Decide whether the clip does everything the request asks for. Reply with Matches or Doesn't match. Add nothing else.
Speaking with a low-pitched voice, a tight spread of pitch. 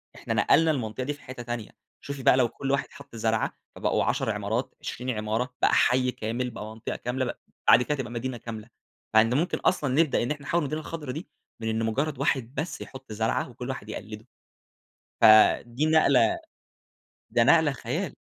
Doesn't match